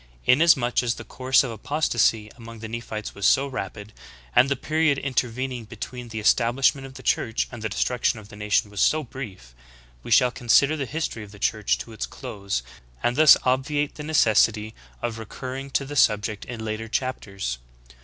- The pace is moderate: Yes, average, 185 wpm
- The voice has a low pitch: Yes, low, 120 Hz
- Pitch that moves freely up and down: No, average, 3.7 semitones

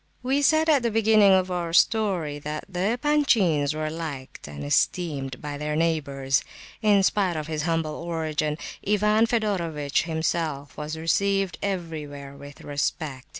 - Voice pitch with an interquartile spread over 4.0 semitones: Yes, average, 5.1 semitones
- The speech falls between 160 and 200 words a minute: No, average, 145 wpm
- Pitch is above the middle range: No, medium, 165 Hz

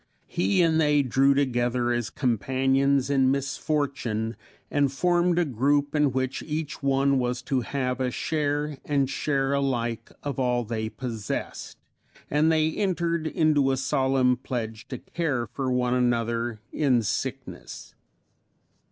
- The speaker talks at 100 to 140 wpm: Yes, slow, 135 wpm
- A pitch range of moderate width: Yes, average, 3.0 semitones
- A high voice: No, low, 135 Hz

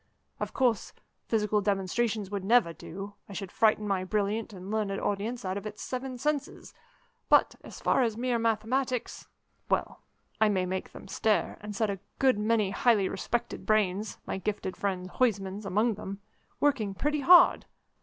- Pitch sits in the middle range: No, high, 210 Hz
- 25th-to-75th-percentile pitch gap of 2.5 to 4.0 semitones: Yes, average, 3.2 semitones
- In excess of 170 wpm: No, average, 160 wpm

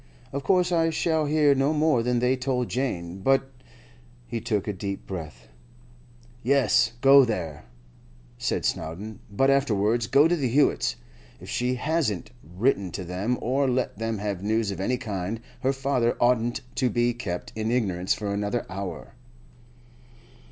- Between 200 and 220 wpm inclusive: No, average, 155 wpm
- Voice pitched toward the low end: Yes, low, 120 Hz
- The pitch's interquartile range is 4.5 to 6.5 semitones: Yes, average, 5.2 semitones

